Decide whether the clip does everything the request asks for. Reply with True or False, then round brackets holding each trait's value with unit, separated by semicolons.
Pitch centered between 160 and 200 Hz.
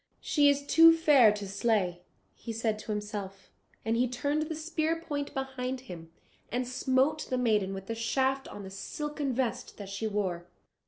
False (245 Hz)